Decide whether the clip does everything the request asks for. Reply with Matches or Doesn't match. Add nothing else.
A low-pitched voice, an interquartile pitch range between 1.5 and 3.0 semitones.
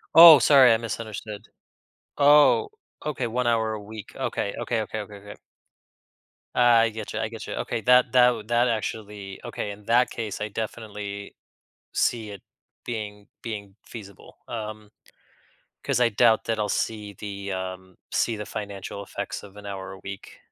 Matches